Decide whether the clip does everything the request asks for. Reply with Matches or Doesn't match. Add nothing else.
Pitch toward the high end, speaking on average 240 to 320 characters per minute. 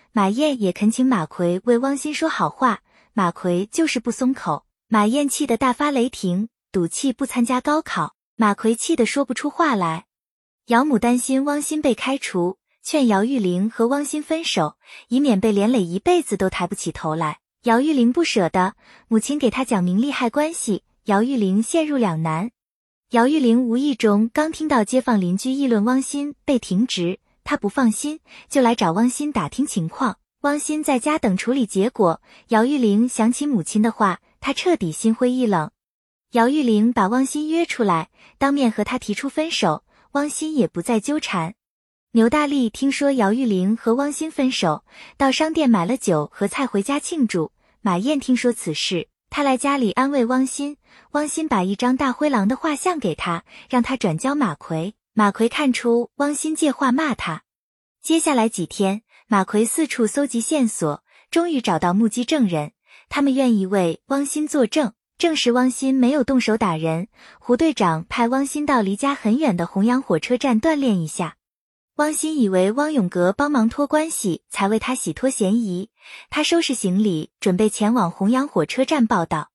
Matches